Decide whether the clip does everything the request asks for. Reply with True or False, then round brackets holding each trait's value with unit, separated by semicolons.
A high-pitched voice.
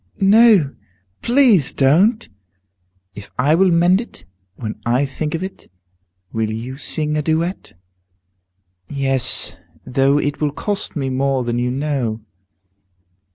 False (145 Hz)